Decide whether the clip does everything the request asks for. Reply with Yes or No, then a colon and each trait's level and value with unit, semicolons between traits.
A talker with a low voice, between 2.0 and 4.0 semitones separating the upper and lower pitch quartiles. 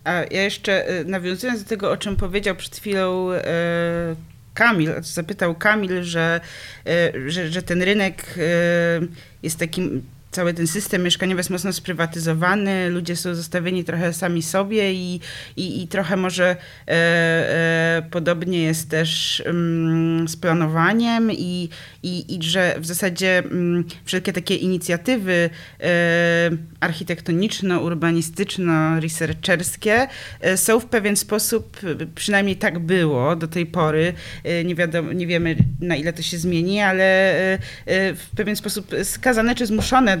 No: medium, 175 Hz; narrow, 2.4 semitones